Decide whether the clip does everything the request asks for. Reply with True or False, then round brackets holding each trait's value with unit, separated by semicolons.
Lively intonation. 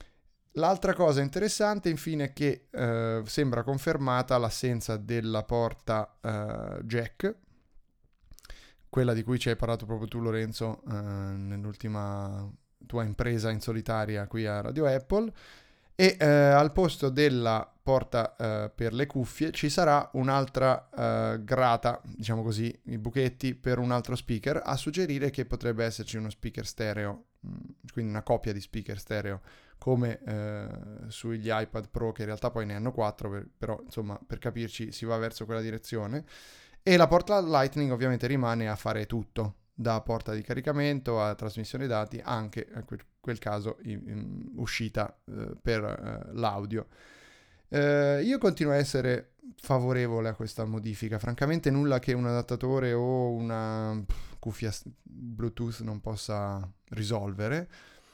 False (3.2 semitones)